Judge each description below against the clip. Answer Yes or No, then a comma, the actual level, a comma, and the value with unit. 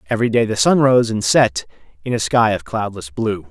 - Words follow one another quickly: Yes, fast, 225 wpm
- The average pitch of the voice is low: Yes, low, 110 Hz